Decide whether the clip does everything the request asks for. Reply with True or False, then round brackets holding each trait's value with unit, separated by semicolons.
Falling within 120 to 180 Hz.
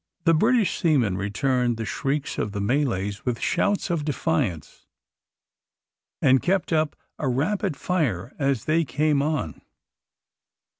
True (140 Hz)